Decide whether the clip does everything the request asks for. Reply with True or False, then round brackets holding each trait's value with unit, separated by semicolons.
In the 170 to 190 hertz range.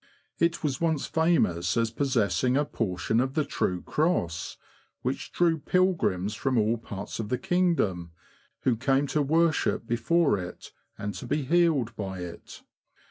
False (125 Hz)